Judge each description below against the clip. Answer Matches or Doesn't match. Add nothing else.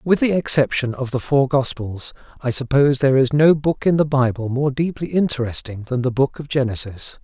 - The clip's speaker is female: Doesn't match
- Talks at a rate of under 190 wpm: Doesn't match